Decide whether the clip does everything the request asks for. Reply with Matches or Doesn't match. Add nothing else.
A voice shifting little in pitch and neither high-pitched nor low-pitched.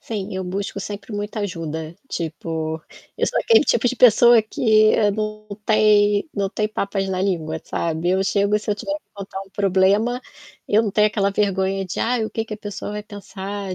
Doesn't match